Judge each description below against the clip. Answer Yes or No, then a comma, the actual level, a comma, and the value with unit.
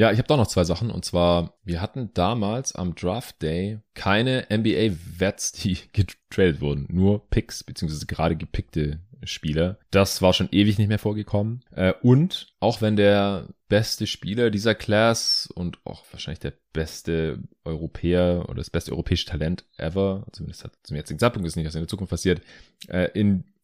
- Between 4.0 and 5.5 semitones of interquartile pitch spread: Yes, average, 4.3 semitones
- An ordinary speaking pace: Yes, average, 175 wpm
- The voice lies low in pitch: Yes, very low, 95 Hz